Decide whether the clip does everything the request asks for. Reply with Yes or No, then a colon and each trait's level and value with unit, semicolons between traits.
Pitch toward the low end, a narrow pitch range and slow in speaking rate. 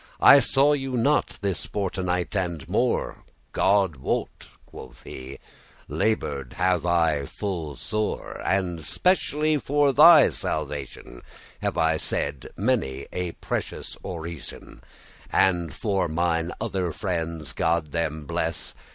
No: very low, 90 Hz; average, 4.9 semitones; slow, 115 wpm